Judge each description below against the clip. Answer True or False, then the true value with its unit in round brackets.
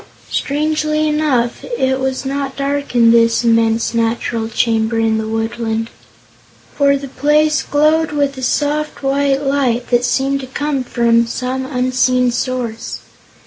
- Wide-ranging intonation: False (3.4 semitones)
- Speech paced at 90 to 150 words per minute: True (140 wpm)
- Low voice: False (260 Hz)